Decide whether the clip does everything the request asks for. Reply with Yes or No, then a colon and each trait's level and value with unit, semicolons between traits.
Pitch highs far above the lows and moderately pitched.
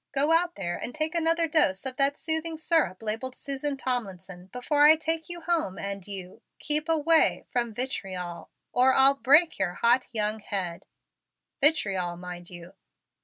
No: wide, 8.4 semitones; very high, 255 Hz